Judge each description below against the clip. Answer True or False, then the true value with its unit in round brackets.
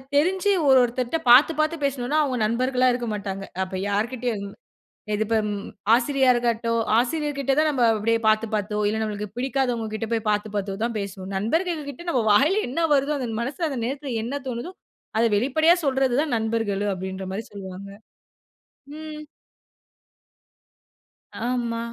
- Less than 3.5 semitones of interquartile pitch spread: False (4.4 semitones)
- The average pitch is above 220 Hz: True (240 Hz)